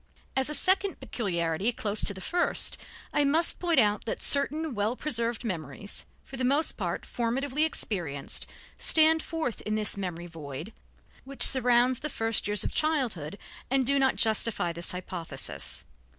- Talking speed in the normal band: Yes, average, 160 wpm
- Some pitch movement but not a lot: No, wide, 7.2 semitones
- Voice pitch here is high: Yes, high, 230 Hz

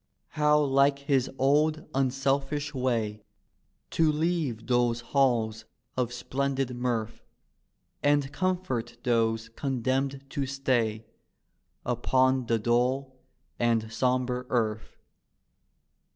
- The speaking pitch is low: Yes, low, 130 Hz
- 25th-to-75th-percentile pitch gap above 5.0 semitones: No, average, 2.8 semitones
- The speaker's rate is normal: No, slow, 95 wpm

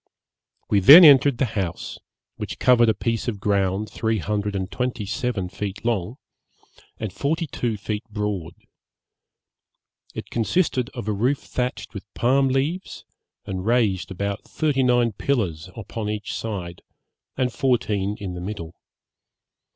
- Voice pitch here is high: No, low, 110 Hz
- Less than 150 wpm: Yes, average, 140 wpm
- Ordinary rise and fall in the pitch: Yes, average, 4.0 semitones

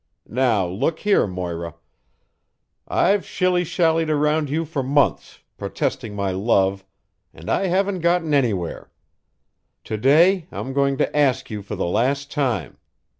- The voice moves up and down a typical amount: No, wide, 8.4 semitones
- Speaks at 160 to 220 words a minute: No, slow, 135 wpm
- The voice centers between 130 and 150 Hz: Yes, medium, 140 Hz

